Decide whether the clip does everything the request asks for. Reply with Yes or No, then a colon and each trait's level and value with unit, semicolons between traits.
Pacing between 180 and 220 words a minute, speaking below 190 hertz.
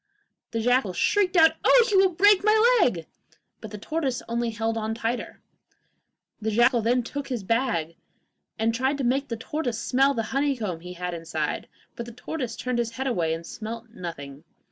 No: average, 190 wpm; high, 235 Hz